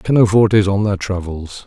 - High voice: No, low, 100 Hz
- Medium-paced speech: Yes, average, 145 wpm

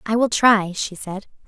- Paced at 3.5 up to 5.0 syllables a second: Yes, 4.3 syllables/s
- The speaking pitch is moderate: No, high, 210 Hz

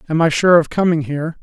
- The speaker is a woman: No, male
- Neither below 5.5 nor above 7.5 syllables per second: Yes, 6.5 syllables/s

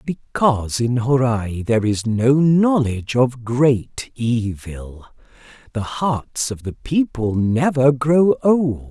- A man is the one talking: Yes, male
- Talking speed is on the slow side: Yes, slow, 120 wpm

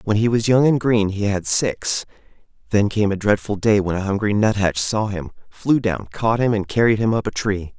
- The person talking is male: Yes, male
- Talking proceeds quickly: Yes, fast, 230 wpm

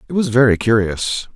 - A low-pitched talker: Yes, low, 115 Hz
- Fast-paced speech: No, average, 175 wpm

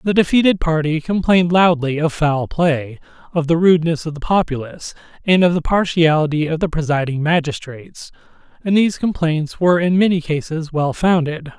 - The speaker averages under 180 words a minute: Yes, average, 160 wpm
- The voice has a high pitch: No, medium, 165 Hz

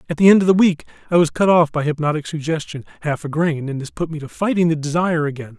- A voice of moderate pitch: Yes, medium, 160 Hz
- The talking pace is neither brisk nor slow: No, fast, 270 wpm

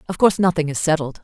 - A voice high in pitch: No, medium, 165 Hz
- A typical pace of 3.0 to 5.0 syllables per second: No, 7.6 syllables/s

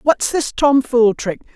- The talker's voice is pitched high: Yes, very high, 250 Hz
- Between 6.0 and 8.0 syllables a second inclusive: No, 3.8 syllables/s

